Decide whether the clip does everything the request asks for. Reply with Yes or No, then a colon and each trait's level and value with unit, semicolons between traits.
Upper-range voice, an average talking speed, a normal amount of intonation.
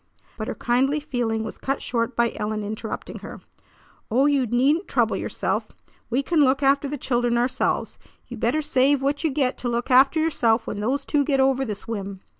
Yes: very high, 255 Hz; average, 195 wpm; average, 3.3 semitones